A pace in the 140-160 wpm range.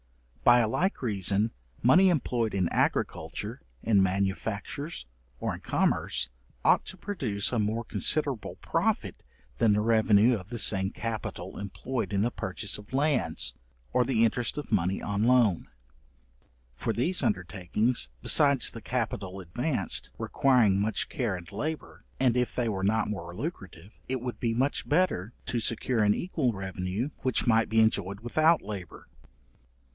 Yes: average, 150 wpm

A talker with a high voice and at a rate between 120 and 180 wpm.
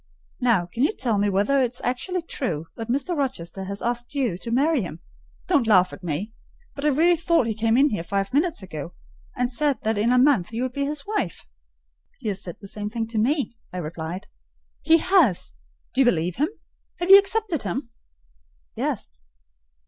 No: high, 240 Hz; average, 200 wpm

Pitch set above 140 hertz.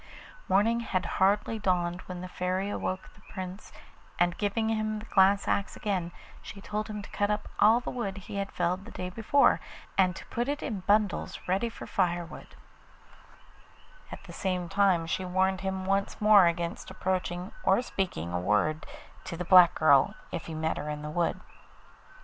Yes: high, 190 Hz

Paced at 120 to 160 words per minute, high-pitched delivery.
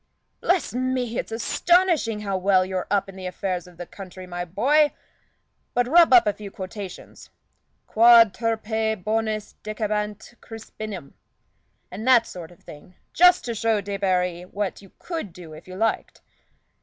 Yes: average, 155 wpm; high, 210 Hz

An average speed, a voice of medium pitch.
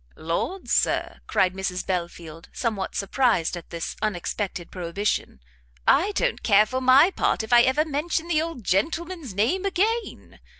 No: average, 145 wpm; high, 230 Hz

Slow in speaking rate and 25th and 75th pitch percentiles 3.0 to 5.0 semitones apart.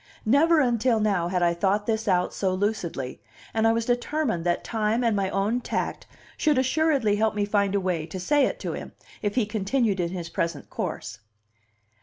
No: average, 195 wpm; average, 4.3 semitones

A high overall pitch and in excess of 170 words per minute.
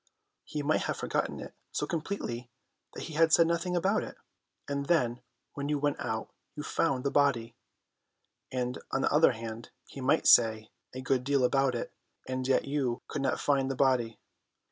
No: low, 135 Hz; average, 180 wpm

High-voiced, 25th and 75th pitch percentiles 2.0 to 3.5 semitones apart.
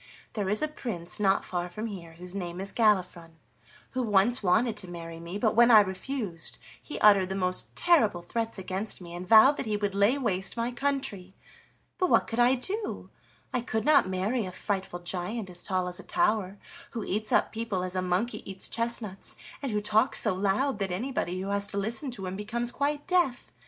No: high, 205 Hz; average, 4.4 semitones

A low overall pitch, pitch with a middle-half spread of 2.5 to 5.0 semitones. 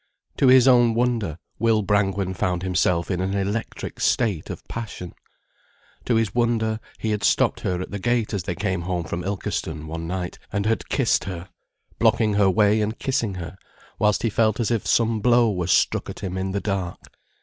Yes: low, 100 Hz; average, 3.6 semitones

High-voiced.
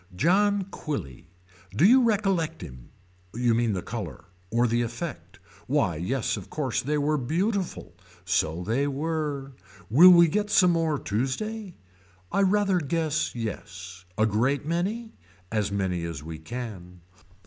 No: low, 135 Hz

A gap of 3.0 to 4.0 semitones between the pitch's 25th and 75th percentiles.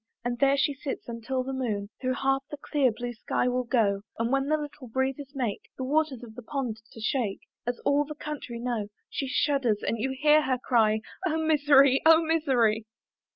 Yes: average, 3.5 semitones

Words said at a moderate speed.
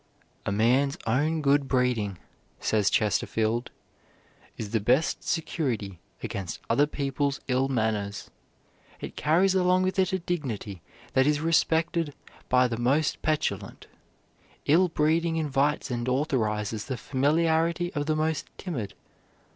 No: slow, 125 wpm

